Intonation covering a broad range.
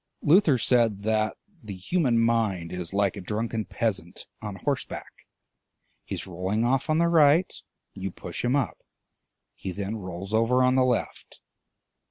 No: average, 4.7 semitones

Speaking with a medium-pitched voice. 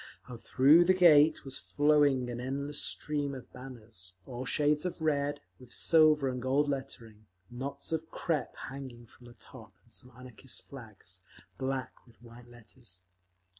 No: low, 130 Hz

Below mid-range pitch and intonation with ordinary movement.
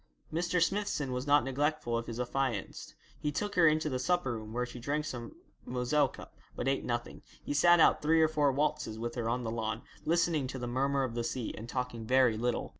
Yes: low, 130 Hz; average, 4.2 semitones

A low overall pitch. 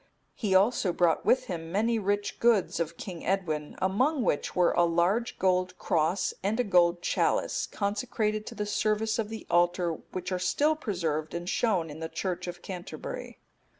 No: medium, 185 Hz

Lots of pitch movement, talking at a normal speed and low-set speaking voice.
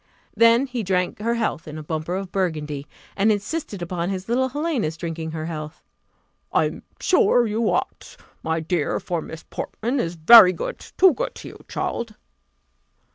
No: wide, 6.4 semitones; average, 170 wpm; medium, 185 Hz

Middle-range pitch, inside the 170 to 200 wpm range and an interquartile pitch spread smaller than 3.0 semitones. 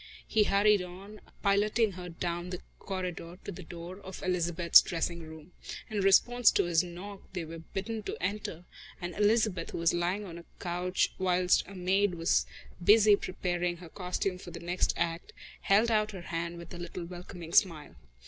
Yes: medium, 180 Hz; average, 175 wpm; narrow, 2.5 semitones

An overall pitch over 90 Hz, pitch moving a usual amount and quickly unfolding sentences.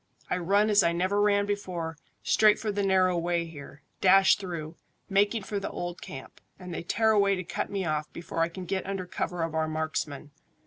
Yes: medium, 185 Hz; average, 3.3 semitones; fast, 210 wpm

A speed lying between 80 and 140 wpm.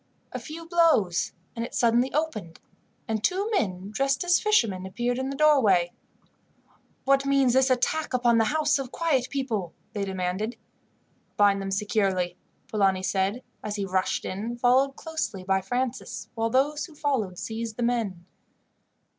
No: average, 155 wpm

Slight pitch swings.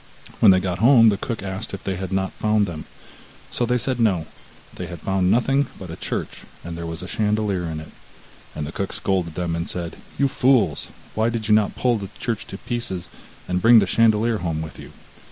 No: average, 4.3 semitones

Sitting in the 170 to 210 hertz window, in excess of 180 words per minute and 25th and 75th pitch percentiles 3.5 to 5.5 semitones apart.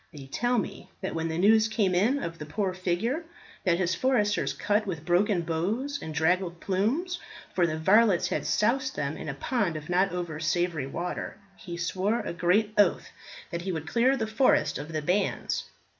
Yes: medium, 185 Hz; average, 190 wpm; average, 4.5 semitones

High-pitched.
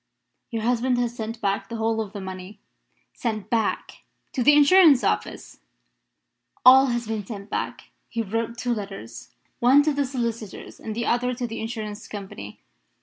Yes: high, 230 Hz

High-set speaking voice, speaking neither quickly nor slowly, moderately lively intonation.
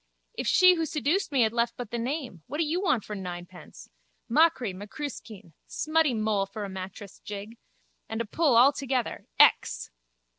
No: high, 235 Hz; average, 175 wpm; wide, 6.5 semitones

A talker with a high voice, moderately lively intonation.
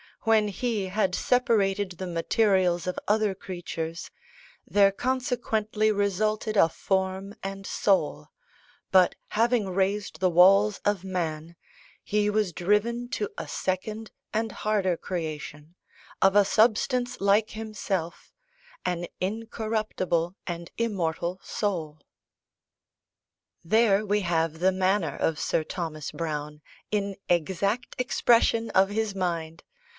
Yes: high, 195 Hz; average, 3.6 semitones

